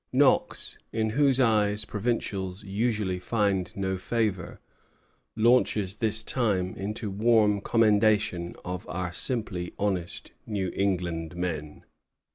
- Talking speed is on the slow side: Yes, slow, 105 wpm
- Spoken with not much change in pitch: No, average, 3.1 semitones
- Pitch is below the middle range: Yes, low, 100 Hz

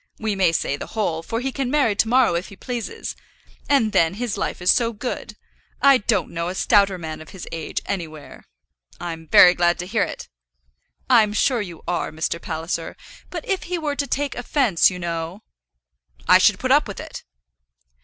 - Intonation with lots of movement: Yes, wide, 6.5 semitones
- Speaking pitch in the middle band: No, high, 200 Hz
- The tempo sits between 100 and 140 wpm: No, average, 195 wpm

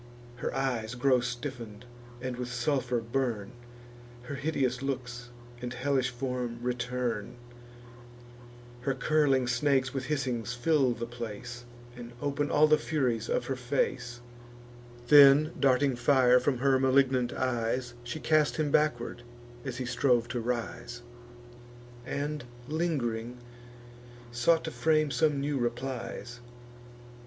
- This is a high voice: No, low, 125 Hz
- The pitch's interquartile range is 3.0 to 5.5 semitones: No, narrow, 2.5 semitones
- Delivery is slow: Yes, slow, 120 wpm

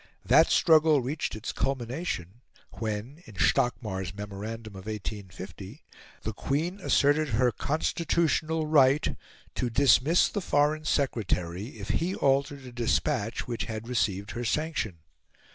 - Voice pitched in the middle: No, low, 125 Hz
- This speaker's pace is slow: Yes, slow, 125 wpm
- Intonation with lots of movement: Yes, wide, 6.2 semitones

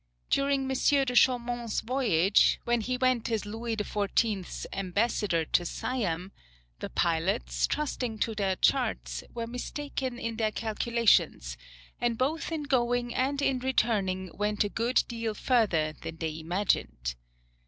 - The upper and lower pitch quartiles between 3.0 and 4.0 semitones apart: No, average, 4.6 semitones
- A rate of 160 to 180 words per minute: No, slow, 135 wpm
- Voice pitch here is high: Yes, high, 225 Hz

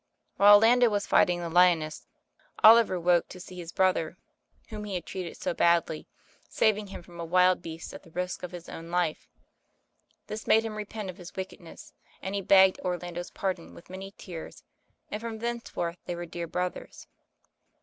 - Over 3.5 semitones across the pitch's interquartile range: No, average, 2.9 semitones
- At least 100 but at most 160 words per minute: No, average, 180 wpm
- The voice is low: No, medium, 180 Hz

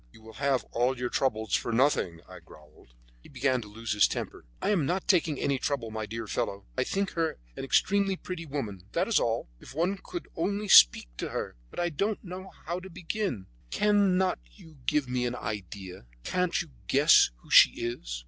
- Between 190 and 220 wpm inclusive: Yes, average, 200 wpm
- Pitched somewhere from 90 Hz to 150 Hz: Yes, medium, 140 Hz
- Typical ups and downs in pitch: No, wide, 8.6 semitones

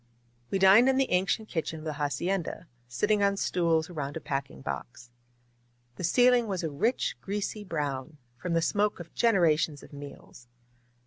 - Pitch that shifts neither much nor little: No, wide, 5.7 semitones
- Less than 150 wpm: No, average, 170 wpm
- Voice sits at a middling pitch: Yes, medium, 170 Hz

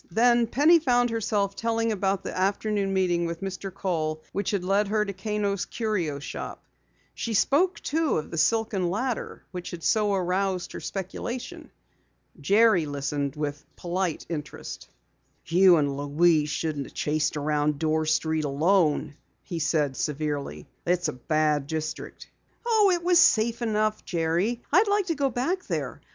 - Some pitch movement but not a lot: No, wide, 6.2 semitones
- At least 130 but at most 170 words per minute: Yes, average, 155 wpm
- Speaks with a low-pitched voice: No, medium, 185 Hz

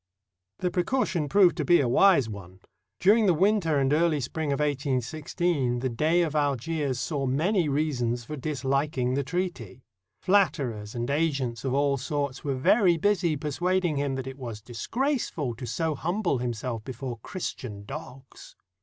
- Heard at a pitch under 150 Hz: Yes, medium, 140 Hz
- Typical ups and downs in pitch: Yes, average, 4.9 semitones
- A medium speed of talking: Yes, average, 155 wpm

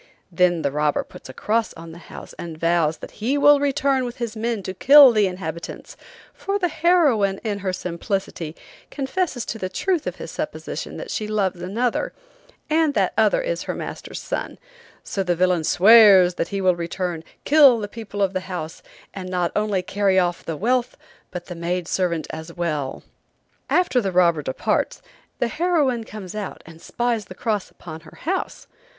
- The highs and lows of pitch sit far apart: Yes, wide, 5.7 semitones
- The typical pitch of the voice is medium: No, high, 195 Hz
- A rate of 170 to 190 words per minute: Yes, average, 180 wpm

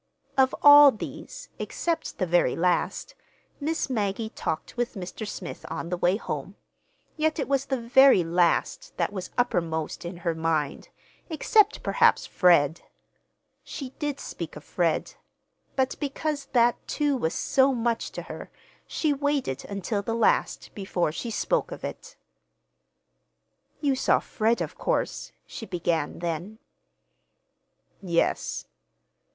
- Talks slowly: Yes, slow, 130 wpm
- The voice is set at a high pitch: Yes, high, 225 Hz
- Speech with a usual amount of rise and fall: No, wide, 7.9 semitones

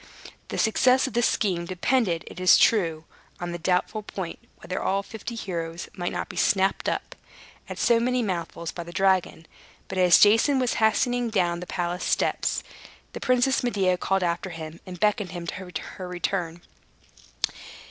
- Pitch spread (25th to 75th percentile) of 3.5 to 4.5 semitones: Yes, average, 4.1 semitones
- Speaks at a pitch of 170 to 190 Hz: Yes, medium, 185 Hz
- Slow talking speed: No, average, 170 wpm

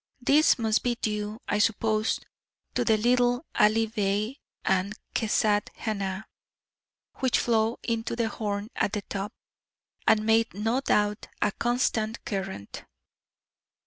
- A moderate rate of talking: No, slow, 125 wpm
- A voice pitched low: No, high, 220 Hz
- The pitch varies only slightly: Yes, narrow, 1.9 semitones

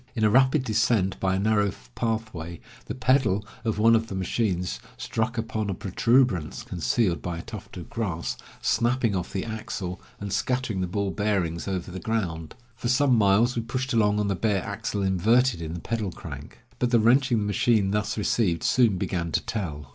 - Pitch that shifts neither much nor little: Yes, average, 3.7 semitones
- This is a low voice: Yes, low, 105 Hz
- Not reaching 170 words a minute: No, average, 190 wpm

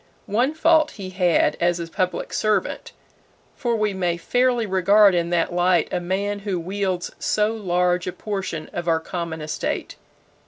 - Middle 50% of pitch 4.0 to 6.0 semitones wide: No, average, 3.2 semitones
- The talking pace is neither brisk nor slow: Yes, average, 160 wpm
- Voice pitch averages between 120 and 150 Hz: No, medium, 185 Hz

